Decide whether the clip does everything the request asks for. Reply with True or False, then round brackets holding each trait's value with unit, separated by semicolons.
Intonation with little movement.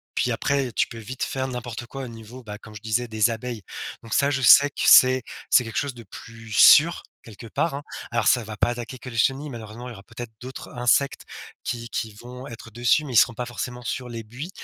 True (2.2 semitones)